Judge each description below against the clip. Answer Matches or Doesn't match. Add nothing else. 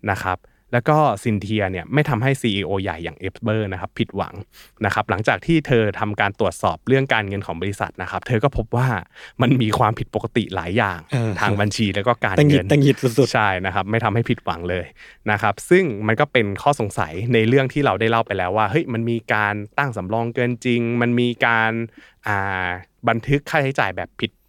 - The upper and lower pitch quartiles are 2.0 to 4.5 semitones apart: Matches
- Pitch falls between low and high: Doesn't match